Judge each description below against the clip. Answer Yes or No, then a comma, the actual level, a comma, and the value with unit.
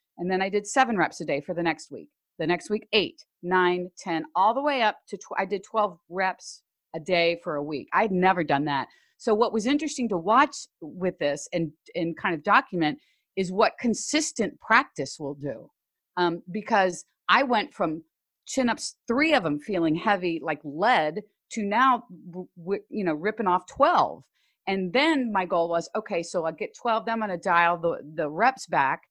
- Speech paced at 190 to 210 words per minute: Yes, average, 200 wpm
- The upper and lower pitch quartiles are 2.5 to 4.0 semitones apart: No, average, 5.1 semitones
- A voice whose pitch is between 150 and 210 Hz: Yes, high, 190 Hz